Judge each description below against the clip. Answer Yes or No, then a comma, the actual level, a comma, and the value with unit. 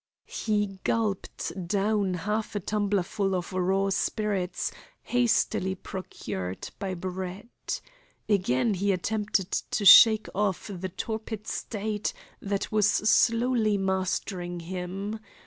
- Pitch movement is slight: Yes, narrow, 2.3 semitones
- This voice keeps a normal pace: No, slow, 105 wpm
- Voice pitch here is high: Yes, high, 200 Hz